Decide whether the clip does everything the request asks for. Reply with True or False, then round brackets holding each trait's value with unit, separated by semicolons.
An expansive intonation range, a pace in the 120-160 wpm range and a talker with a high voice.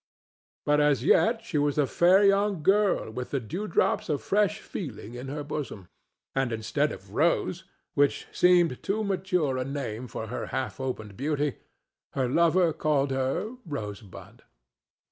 False (5.9 semitones; 145 wpm; 145 Hz)